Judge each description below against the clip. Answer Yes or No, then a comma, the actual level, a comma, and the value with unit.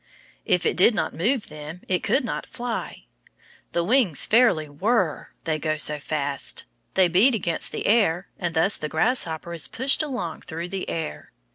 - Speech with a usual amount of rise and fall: No, wide, 6.2 semitones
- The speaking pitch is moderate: Yes, medium, 175 Hz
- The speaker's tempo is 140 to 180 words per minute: Yes, average, 170 wpm